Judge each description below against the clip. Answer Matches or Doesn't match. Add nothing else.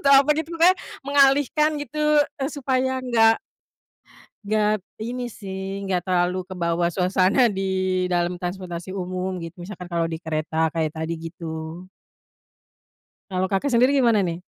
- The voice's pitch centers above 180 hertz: Matches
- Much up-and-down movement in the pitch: Matches